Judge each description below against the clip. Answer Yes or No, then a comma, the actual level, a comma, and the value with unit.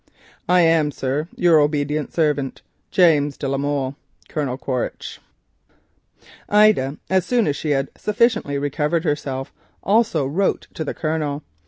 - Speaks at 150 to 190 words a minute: No, average, 140 wpm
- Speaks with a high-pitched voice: No, medium, 150 Hz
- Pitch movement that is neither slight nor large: Yes, average, 3.3 semitones